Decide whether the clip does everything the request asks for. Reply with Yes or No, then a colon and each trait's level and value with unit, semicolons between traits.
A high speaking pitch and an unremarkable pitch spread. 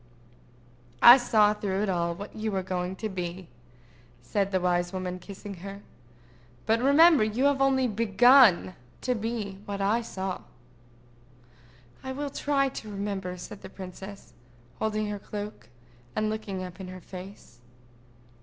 Yes: high, 205 Hz; average, 3.3 semitones